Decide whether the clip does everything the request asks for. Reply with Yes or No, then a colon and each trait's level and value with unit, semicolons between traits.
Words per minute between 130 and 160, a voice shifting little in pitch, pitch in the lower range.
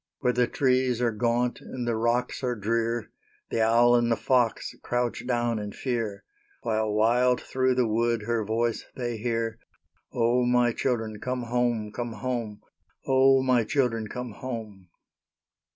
Yes: average, 150 wpm; narrow, 1.7 semitones; low, 120 Hz